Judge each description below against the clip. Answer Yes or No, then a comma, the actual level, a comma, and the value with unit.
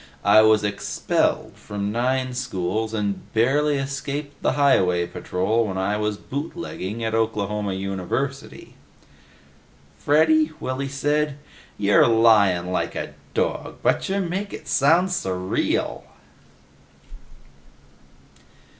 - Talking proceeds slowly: Yes, slow, 105 wpm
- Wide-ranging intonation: Yes, wide, 5.9 semitones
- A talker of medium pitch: No, low, 115 Hz